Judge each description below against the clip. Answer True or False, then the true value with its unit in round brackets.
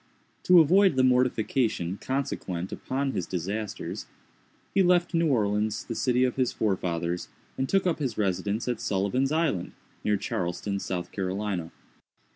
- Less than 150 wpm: True (140 wpm)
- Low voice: True (110 Hz)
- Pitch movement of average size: False (6.0 semitones)